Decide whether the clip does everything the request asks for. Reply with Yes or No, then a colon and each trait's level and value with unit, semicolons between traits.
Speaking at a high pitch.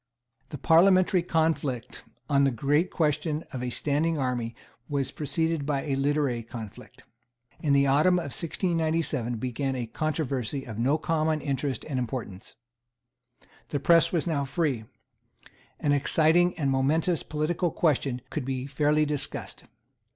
No: medium, 145 Hz